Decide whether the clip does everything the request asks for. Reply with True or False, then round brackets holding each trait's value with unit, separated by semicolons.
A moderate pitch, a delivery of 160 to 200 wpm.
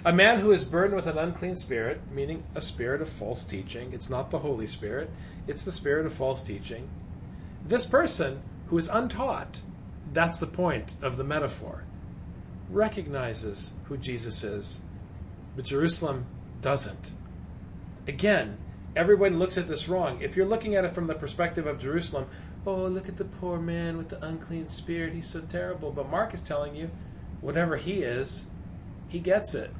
True (150 Hz; 170 wpm)